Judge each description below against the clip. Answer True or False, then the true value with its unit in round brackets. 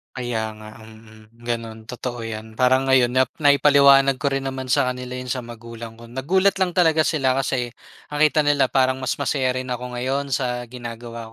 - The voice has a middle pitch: False (125 Hz)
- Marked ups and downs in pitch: False (2.6 semitones)